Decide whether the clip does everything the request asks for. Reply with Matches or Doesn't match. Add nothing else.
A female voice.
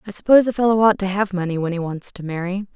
Matches